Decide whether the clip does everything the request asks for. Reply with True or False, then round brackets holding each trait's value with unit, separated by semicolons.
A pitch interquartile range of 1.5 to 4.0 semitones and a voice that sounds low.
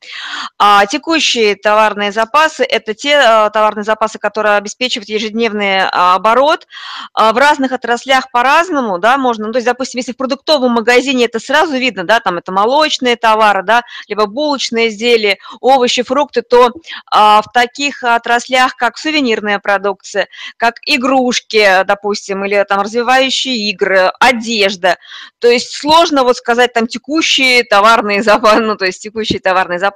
False (3.5 semitones; 235 Hz)